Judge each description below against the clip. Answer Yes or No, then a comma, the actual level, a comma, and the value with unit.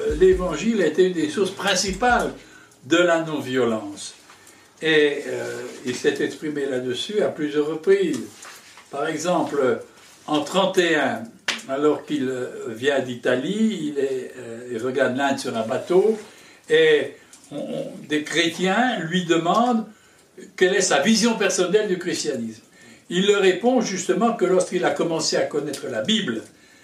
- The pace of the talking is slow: Yes, slow, 135 wpm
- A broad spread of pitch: Yes, wide, 6.6 semitones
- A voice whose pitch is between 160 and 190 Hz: Yes, medium, 185 Hz